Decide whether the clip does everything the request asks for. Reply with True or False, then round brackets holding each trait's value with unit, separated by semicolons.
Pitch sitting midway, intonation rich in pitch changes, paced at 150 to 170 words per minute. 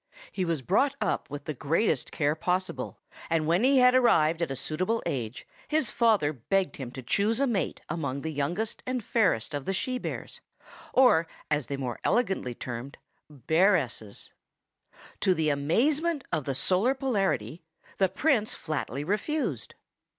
True (170 Hz; 8.0 semitones; 160 wpm)